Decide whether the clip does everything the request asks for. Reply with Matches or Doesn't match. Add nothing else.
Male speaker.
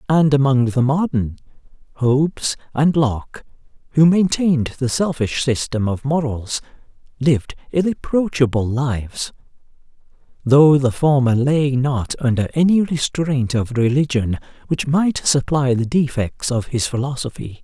Matches